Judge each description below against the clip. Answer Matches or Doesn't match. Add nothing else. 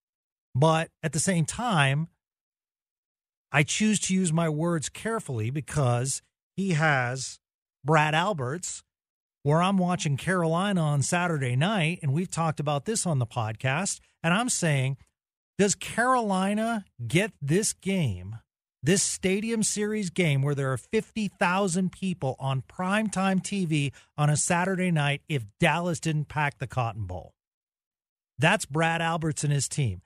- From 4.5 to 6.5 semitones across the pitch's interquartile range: Matches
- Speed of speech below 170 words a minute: Matches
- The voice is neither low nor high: Matches